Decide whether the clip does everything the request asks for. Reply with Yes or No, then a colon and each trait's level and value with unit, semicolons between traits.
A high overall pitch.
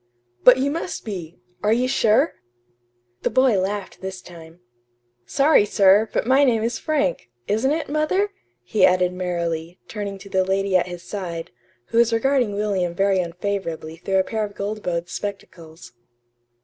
Yes: high, 200 Hz